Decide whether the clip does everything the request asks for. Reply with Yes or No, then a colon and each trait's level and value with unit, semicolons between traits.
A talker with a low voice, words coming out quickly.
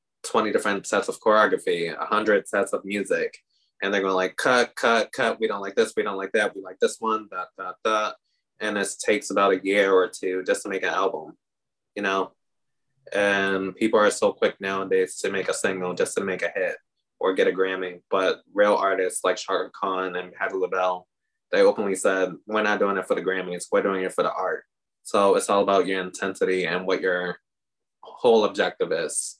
Yes: low, 110 Hz; fast, 210 wpm